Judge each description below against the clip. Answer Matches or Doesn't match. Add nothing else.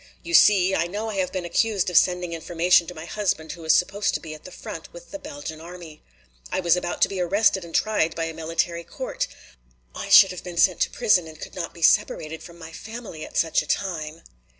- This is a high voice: Doesn't match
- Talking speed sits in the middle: Doesn't match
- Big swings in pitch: Doesn't match